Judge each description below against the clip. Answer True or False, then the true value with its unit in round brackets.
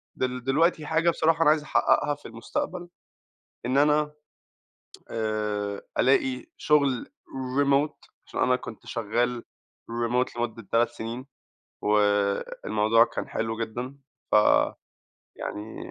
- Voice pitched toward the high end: False (120 Hz)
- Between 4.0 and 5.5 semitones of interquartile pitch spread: True (4.5 semitones)